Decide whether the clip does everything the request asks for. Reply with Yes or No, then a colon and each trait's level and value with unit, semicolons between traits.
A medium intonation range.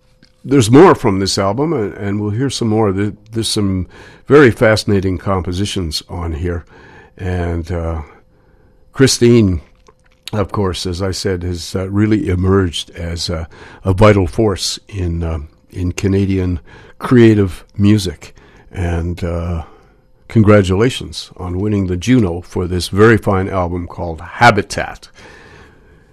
Yes: average, 3.2 semitones